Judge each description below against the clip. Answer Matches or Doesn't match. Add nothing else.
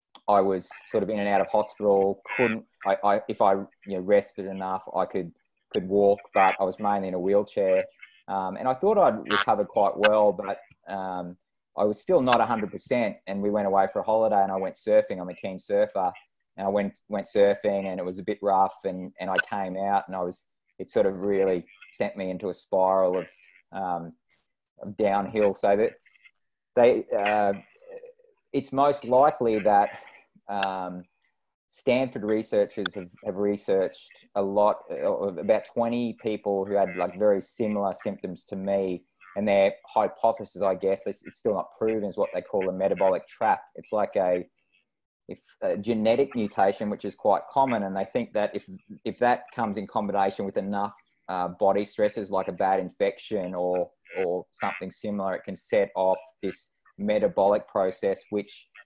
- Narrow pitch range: Matches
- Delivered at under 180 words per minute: Doesn't match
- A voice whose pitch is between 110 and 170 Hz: Doesn't match